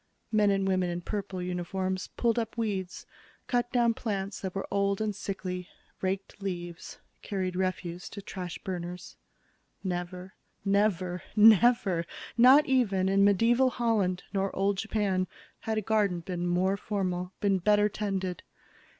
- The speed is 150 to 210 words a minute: No, average, 140 wpm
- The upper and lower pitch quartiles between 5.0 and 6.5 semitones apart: No, narrow, 2.6 semitones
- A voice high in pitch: Yes, high, 195 Hz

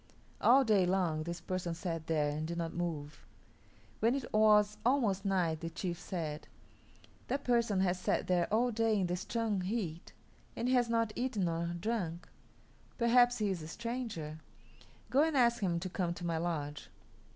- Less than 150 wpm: No, average, 175 wpm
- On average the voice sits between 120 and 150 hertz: No, medium, 185 Hz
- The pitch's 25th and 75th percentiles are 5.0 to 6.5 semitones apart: Yes, wide, 5.4 semitones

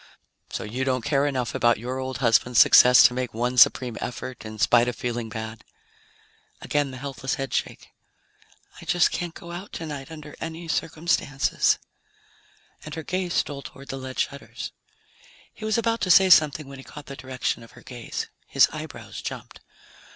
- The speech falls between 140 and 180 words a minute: Yes, average, 175 wpm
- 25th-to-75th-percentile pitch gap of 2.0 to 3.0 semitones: No, average, 4.0 semitones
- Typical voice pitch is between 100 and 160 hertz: Yes, low, 135 Hz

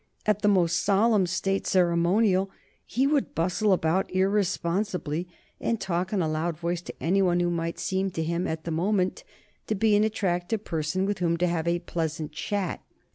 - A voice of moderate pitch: Yes, medium, 180 Hz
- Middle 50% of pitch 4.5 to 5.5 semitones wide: No, average, 2.8 semitones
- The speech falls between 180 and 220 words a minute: Yes, average, 185 wpm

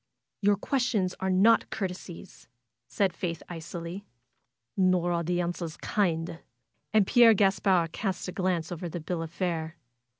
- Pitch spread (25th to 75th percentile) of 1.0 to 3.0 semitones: Yes, narrow, 2.6 semitones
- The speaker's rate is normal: Yes, average, 145 wpm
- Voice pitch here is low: No, medium, 180 Hz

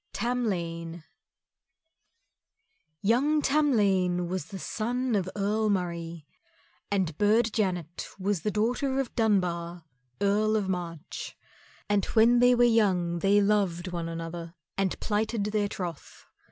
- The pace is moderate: No, slow, 115 wpm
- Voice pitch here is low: No, high, 200 Hz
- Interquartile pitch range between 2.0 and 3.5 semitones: No, average, 4.1 semitones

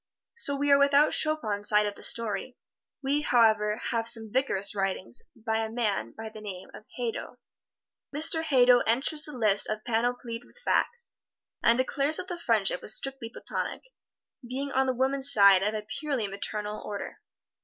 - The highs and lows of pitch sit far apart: No, average, 4.7 semitones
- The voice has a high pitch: Yes, high, 235 Hz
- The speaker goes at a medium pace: Yes, average, 165 wpm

